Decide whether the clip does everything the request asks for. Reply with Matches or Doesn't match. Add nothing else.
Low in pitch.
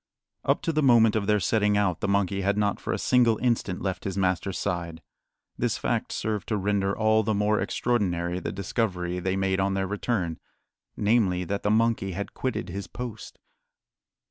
Matches